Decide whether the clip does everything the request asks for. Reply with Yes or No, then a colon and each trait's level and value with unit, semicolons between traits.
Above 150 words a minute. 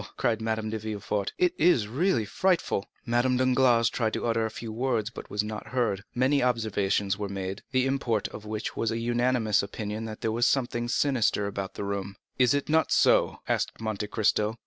Yes: average, 195 wpm